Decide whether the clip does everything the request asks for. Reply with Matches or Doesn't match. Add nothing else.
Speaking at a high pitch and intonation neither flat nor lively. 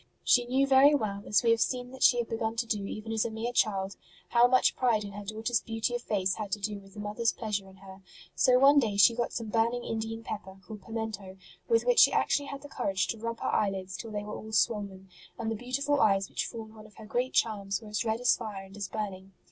Matches